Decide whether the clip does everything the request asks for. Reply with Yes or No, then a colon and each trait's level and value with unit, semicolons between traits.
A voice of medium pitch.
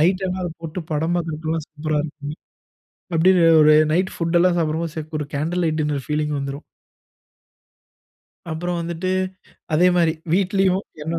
Yes: medium, 165 Hz